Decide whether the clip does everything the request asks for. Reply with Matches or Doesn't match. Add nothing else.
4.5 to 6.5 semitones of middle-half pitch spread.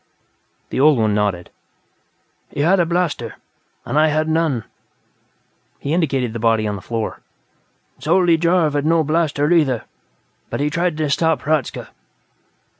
Matches